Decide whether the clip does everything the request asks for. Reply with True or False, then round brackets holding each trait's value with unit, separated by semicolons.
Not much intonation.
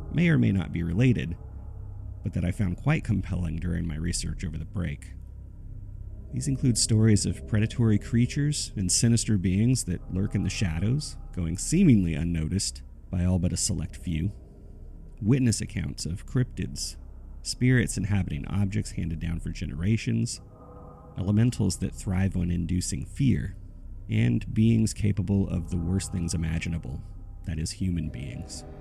False (4.2 semitones)